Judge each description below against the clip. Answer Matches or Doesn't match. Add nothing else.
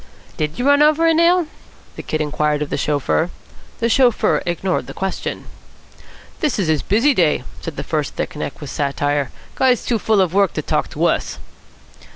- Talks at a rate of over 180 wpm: Matches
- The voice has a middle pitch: Matches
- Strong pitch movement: Matches